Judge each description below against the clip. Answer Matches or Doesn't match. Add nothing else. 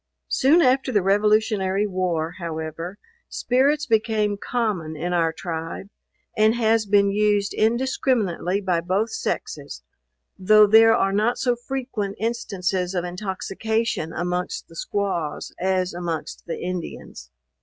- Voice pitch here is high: Matches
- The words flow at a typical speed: Doesn't match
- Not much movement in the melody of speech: Doesn't match